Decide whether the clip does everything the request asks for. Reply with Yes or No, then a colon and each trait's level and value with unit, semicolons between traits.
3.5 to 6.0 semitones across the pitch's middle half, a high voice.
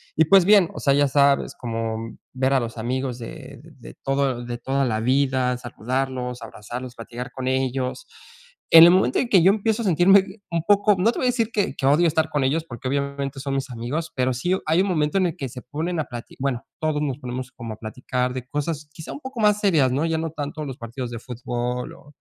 No: average, 4.6 semitones; low, 135 Hz